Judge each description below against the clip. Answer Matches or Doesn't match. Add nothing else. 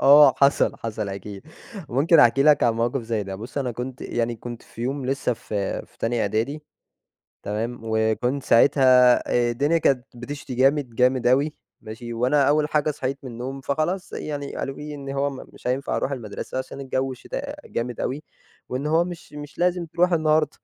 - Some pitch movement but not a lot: Matches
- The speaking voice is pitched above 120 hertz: Matches